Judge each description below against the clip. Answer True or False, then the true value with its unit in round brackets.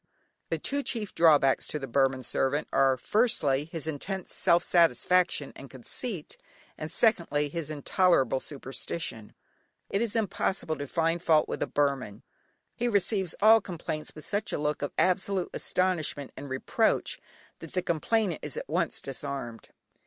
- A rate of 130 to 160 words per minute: True (150 wpm)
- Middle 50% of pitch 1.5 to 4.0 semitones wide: False (5.0 semitones)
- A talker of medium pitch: True (160 Hz)